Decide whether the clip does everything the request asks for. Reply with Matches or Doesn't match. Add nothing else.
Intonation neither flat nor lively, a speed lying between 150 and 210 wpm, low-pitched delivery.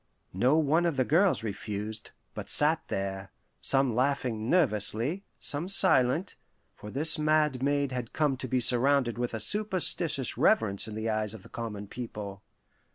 Doesn't match